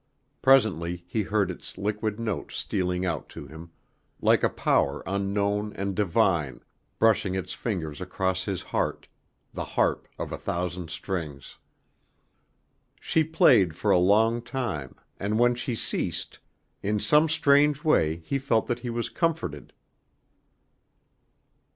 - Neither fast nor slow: No, slow, 130 wpm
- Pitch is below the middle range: Yes, low, 100 Hz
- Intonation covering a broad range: No, average, 4.8 semitones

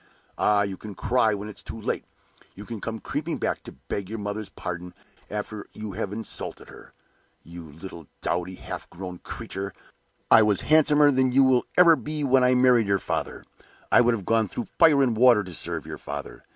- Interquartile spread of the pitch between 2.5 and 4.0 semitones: No, average, 4.6 semitones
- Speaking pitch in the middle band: No, low, 110 Hz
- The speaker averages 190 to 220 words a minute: Yes, average, 195 wpm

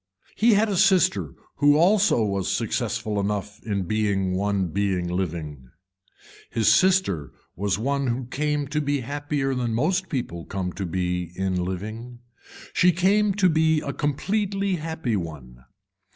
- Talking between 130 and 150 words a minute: Yes, average, 145 wpm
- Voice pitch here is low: Yes, low, 115 Hz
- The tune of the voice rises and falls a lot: Yes, wide, 9.0 semitones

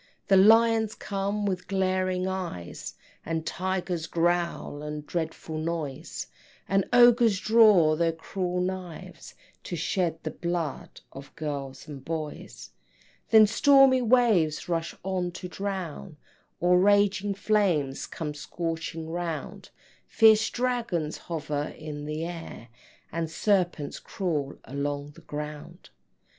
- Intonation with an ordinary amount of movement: Yes, average, 4.1 semitones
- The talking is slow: Yes, slow, 115 wpm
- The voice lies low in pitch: No, medium, 175 Hz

